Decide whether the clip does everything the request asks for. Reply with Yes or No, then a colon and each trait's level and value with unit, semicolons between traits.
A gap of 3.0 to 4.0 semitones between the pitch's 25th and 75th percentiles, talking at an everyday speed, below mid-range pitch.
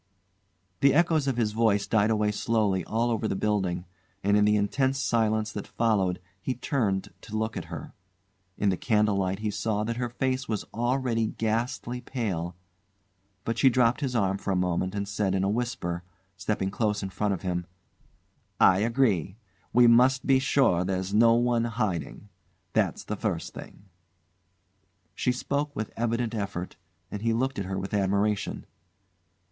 Yes: average, 3.4 semitones; average, 170 wpm; low, 110 Hz